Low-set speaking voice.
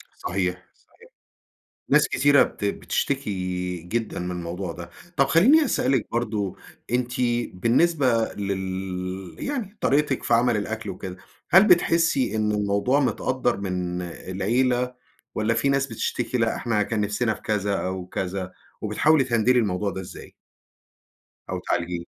Yes: low, 110 Hz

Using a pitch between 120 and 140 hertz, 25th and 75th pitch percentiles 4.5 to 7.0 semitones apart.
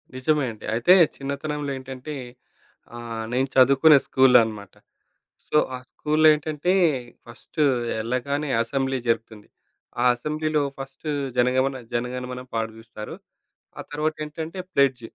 No: low, 135 Hz; average, 3.8 semitones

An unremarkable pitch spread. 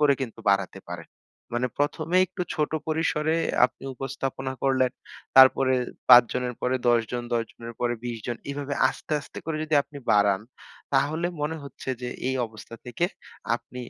Yes: average, 3.5 semitones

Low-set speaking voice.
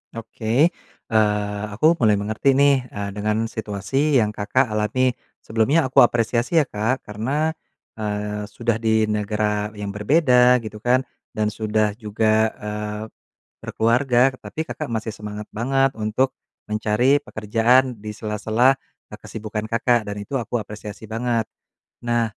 Yes: low, 110 Hz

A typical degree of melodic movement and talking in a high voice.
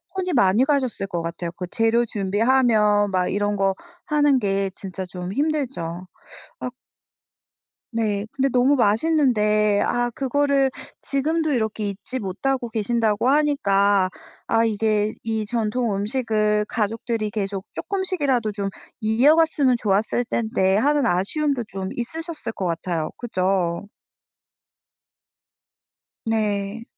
Yes: average, 4.7 semitones; high, 220 Hz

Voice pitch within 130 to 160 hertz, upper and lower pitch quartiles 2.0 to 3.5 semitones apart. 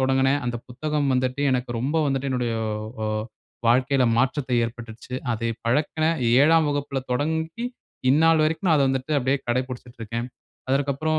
Yes: low, 135 Hz; average, 3.2 semitones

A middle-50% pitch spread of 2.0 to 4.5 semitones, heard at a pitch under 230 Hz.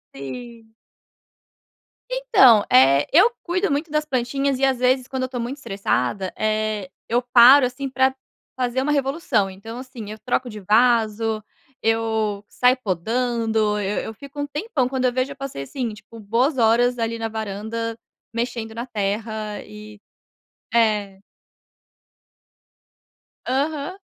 No: average, 3.5 semitones; high, 235 Hz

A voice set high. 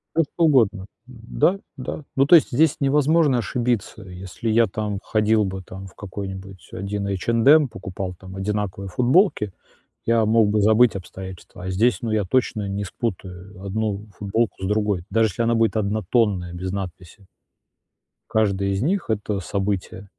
No: low, 105 Hz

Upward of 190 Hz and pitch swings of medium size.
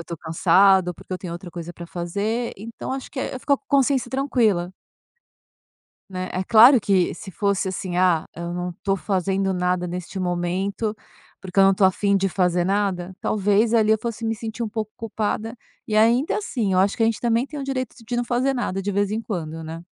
Yes: high, 200 Hz; average, 4.0 semitones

